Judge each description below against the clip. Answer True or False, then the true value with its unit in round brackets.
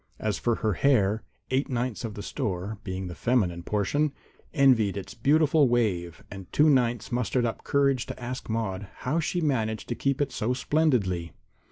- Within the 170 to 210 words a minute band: True (175 wpm)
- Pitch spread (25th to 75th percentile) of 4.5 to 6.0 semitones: True (5.3 semitones)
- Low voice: True (120 Hz)